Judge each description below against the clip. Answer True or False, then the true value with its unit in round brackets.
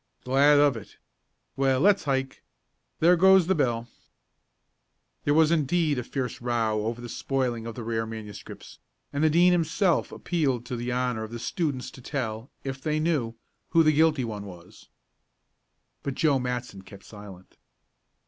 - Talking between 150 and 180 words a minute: True (160 wpm)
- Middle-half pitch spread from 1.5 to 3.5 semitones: False (5.0 semitones)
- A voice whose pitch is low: True (130 Hz)